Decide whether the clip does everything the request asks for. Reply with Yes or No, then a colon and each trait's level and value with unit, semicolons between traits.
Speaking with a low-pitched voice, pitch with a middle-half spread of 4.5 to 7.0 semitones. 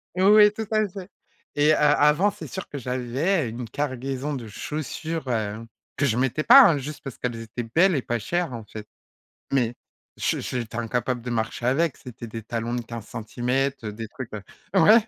Yes: low, 130 Hz; average, 4.9 semitones